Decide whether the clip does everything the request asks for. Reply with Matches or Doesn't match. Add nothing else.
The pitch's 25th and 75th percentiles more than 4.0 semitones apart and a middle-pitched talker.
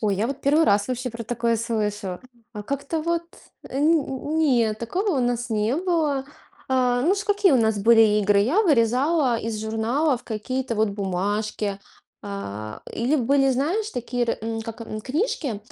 Doesn't match